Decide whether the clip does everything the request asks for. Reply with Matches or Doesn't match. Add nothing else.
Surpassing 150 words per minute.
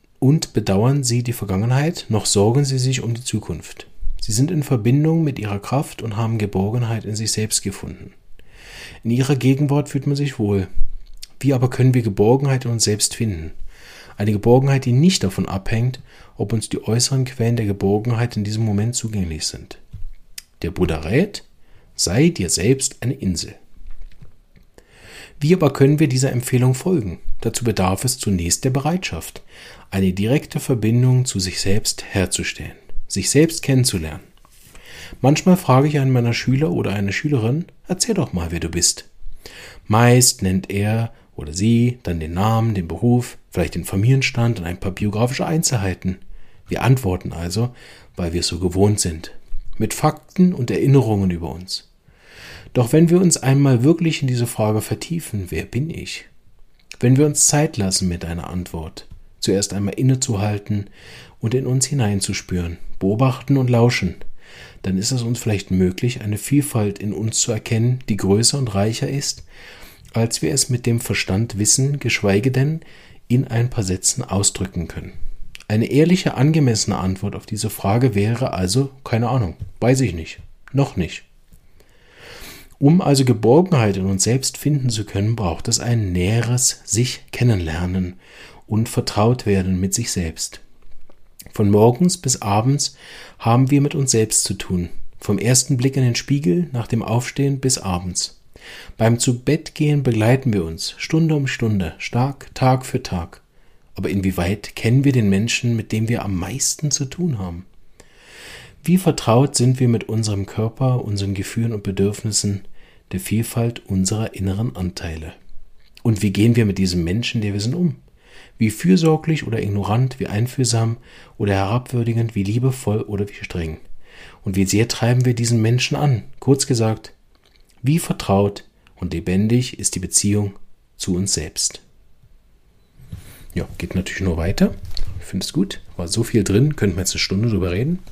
Matches